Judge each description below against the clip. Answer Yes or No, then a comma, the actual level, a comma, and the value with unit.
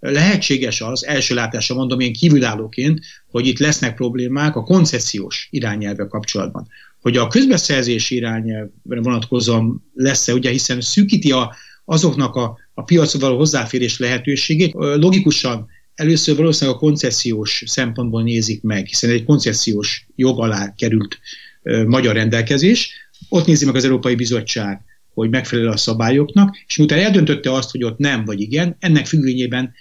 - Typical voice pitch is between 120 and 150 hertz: Yes, low, 130 Hz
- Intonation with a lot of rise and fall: No, average, 4.4 semitones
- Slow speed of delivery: No, average, 140 wpm